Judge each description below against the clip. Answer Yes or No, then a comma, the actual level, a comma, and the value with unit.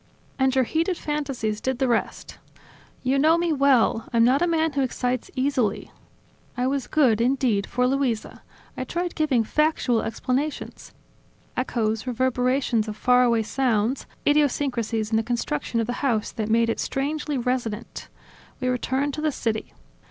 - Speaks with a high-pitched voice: Yes, very high, 255 Hz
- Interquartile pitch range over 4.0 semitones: No, average, 3.4 semitones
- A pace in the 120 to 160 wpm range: Yes, average, 155 wpm